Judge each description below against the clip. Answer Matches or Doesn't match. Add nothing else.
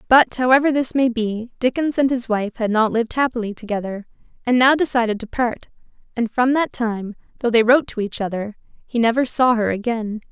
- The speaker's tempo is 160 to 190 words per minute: Doesn't match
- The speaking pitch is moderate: Doesn't match